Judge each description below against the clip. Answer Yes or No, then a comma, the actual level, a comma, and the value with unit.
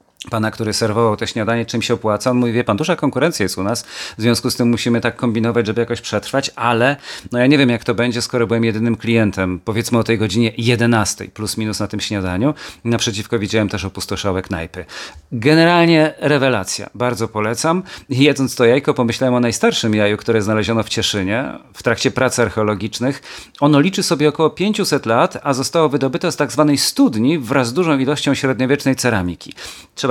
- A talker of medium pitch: No, low, 120 Hz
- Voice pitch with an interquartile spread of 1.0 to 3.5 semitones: No, average, 3.9 semitones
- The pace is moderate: No, fast, 180 wpm